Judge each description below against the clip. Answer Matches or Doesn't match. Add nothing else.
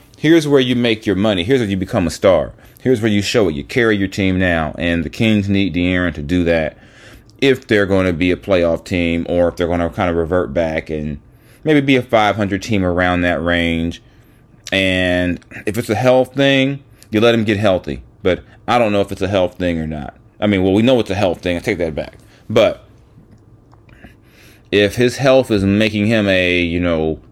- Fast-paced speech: Matches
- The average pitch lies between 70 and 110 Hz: Matches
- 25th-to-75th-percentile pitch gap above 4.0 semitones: Matches